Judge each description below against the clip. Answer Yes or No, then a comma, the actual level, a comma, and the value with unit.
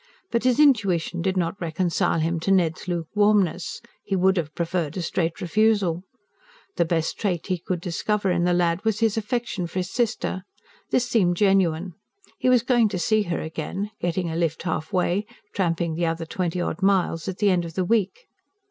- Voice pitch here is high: No, medium, 180 Hz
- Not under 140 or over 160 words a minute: No, average, 190 wpm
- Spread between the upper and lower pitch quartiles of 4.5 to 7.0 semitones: No, average, 3.5 semitones